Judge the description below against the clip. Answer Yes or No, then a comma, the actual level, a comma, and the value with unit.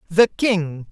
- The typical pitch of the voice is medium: Yes, medium, 180 Hz